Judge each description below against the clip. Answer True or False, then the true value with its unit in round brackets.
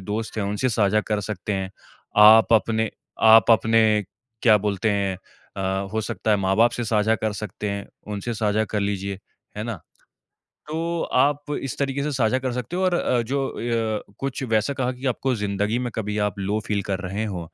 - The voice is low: True (110 Hz)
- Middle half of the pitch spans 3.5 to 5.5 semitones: False (3.0 semitones)